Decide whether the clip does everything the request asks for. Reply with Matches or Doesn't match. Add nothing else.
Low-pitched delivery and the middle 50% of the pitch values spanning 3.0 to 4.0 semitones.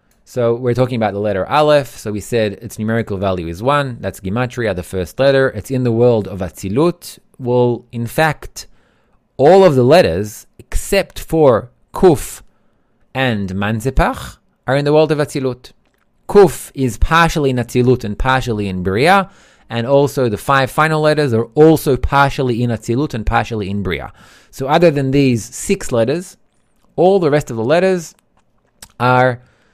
Doesn't match